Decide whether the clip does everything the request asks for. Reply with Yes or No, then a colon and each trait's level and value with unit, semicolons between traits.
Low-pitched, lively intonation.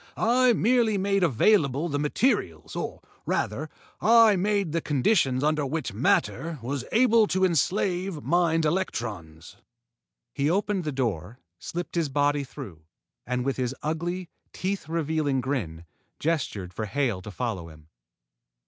No: medium, 150 Hz; wide, 7.0 semitones